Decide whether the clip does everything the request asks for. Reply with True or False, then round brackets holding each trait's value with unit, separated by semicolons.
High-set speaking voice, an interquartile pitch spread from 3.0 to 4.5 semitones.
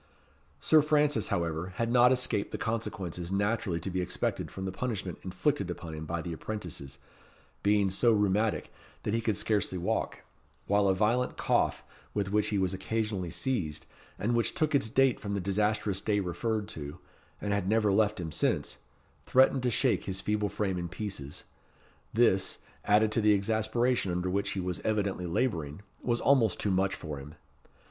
False (100 Hz; 3.6 semitones)